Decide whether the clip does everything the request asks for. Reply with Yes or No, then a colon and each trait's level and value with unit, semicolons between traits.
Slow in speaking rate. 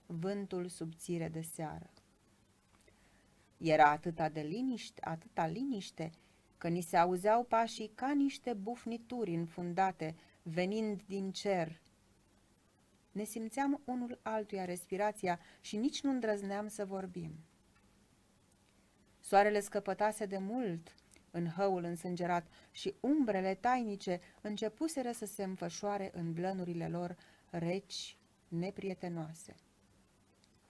Yes: slow, 100 wpm